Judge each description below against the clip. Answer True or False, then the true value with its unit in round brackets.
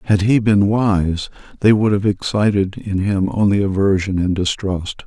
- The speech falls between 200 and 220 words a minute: False (165 wpm)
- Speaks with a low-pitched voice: True (100 Hz)